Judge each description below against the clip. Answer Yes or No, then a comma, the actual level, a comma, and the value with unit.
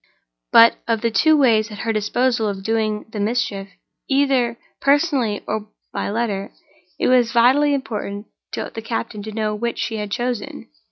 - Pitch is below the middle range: No, high, 225 Hz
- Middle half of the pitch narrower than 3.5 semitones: Yes, average, 2.8 semitones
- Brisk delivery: No, average, 155 wpm